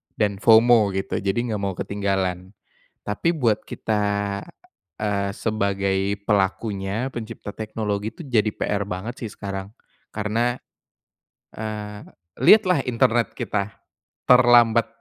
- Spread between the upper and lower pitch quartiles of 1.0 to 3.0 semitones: Yes, narrow, 2.5 semitones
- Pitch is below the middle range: Yes, low, 105 Hz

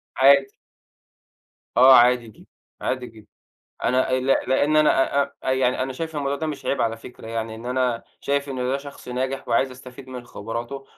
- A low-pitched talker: Yes, low, 130 Hz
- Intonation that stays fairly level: Yes, narrow, 2.0 semitones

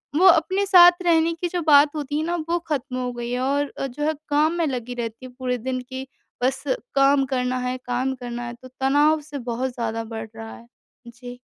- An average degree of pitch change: Yes, average, 3.6 semitones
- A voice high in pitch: Yes, very high, 265 Hz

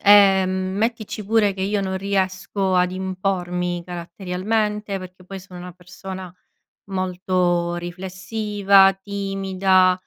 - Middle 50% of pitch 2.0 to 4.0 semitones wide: No, narrow, 1.5 semitones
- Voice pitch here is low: No, high, 190 Hz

